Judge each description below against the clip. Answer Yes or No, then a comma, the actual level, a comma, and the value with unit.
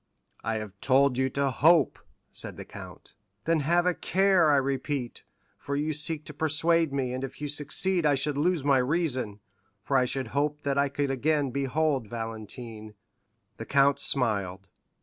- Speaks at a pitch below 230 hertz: Yes, medium, 140 Hz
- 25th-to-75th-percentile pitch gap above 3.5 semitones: No, average, 3.2 semitones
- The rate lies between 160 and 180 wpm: Yes, average, 170 wpm